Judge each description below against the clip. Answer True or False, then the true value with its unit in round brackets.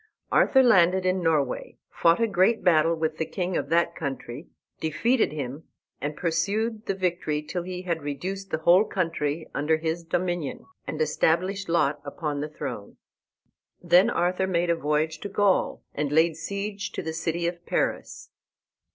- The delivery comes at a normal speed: True (160 wpm)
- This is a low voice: False (170 Hz)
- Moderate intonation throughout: True (3.2 semitones)